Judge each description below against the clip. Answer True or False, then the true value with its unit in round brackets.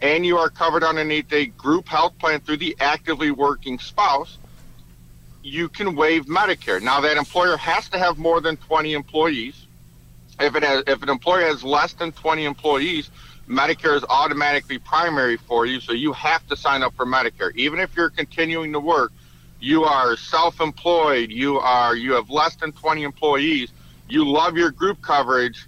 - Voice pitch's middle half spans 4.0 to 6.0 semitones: True (4.4 semitones)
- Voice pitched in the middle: True (150 Hz)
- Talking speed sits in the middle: True (175 wpm)